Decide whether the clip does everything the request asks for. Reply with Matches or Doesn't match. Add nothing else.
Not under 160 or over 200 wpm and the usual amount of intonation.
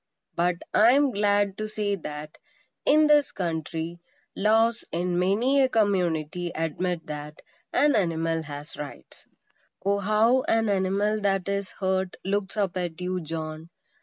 Doesn't match